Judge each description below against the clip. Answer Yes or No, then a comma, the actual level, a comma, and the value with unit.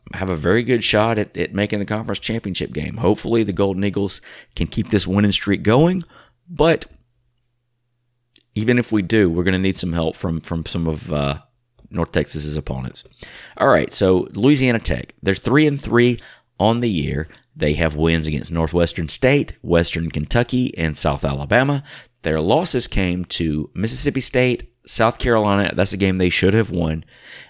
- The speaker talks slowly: No, average, 170 wpm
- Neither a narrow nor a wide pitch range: No, wide, 6.1 semitones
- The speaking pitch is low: Yes, low, 100 Hz